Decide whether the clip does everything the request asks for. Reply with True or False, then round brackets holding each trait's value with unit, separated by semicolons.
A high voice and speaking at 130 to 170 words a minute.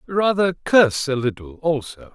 False (150 Hz; 140 wpm)